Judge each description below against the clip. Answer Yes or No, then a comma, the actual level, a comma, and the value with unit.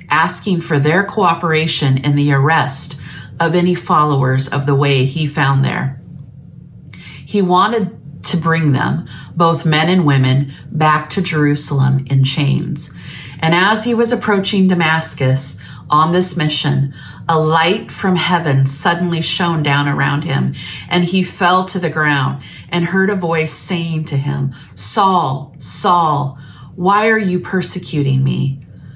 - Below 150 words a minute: Yes, average, 140 wpm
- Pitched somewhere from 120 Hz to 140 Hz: No, medium, 155 Hz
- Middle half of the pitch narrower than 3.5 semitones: No, average, 4.1 semitones